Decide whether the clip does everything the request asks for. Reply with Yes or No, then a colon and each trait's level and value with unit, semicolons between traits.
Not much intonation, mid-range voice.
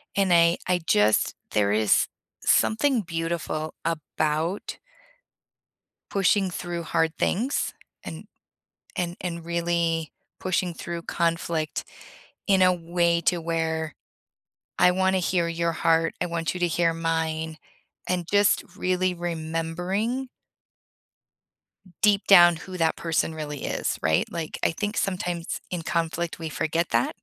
Yes: narrow, 1.8 semitones; medium, 170 Hz